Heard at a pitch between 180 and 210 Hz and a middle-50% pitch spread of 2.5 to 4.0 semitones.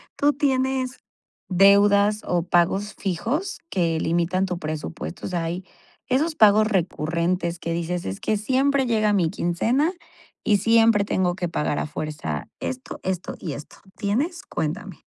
No: high, 190 Hz; average, 5.0 semitones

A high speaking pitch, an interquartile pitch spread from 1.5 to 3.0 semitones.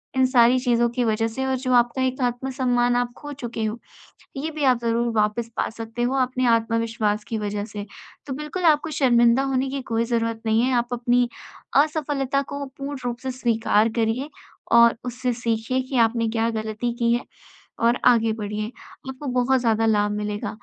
Yes: high, 240 Hz; narrow, 2.5 semitones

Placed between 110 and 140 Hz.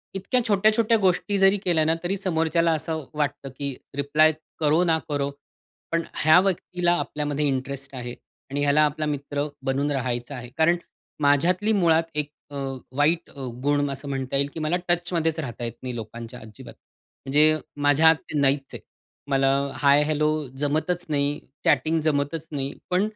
No: medium, 150 Hz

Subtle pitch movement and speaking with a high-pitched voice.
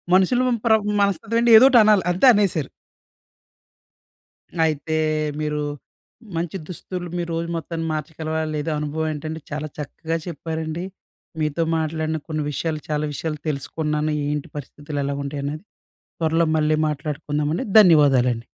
No: narrow, 2.0 semitones; medium, 155 Hz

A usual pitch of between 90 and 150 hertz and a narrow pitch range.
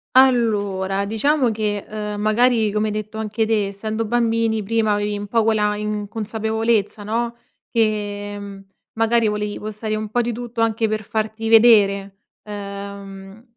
No: high, 215 Hz; narrow, 1.6 semitones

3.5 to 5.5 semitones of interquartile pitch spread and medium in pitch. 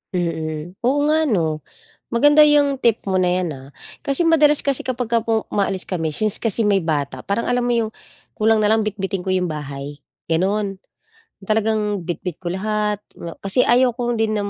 No: average, 5.0 semitones; high, 210 Hz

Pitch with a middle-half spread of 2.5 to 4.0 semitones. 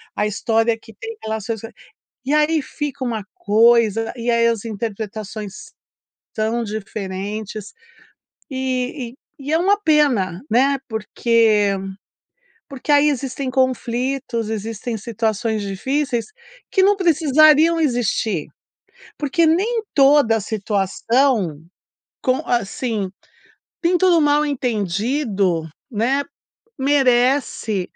No: average, 4.7 semitones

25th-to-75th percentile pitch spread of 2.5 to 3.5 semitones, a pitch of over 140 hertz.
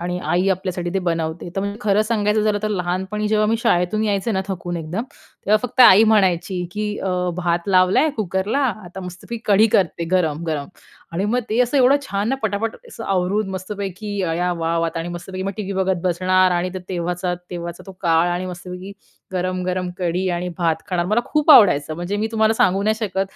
Yes: average, 3.1 semitones; medium, 185 Hz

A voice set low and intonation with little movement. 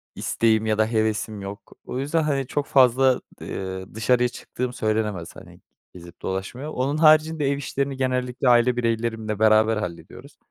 No: low, 120 Hz; average, 3.7 semitones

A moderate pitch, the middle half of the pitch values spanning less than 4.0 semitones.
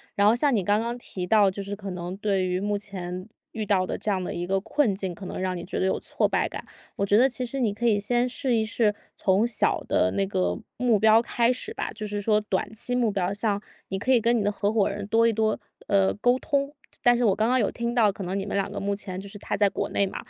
No: high, 205 Hz; average, 3.0 semitones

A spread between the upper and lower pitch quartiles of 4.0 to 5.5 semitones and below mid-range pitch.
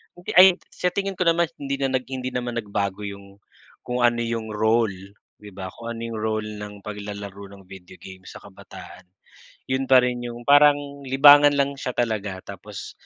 Yes: average, 4.7 semitones; low, 115 Hz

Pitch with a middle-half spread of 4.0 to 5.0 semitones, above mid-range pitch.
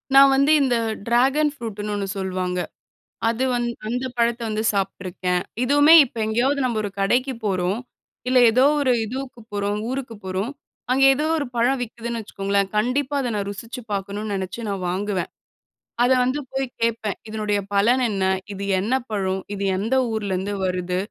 Yes: average, 4.3 semitones; high, 220 Hz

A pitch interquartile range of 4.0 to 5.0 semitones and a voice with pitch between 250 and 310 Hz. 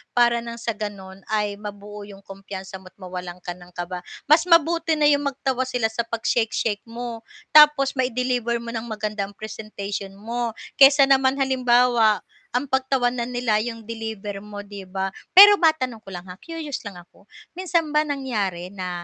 No: average, 4.5 semitones; high, 225 Hz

